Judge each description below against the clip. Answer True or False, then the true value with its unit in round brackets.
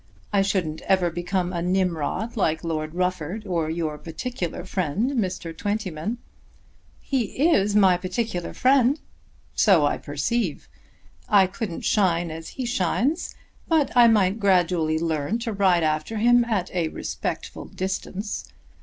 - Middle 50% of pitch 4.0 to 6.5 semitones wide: True (4.8 semitones)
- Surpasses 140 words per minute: False (135 wpm)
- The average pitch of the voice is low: False (185 Hz)